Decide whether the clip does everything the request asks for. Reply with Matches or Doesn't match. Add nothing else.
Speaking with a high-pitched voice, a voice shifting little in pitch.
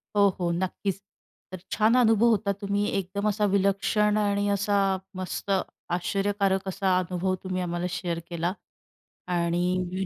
Matches